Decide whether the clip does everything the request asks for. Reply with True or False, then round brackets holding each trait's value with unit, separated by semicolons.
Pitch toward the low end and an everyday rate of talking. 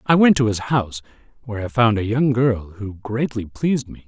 False (115 Hz; 220 wpm)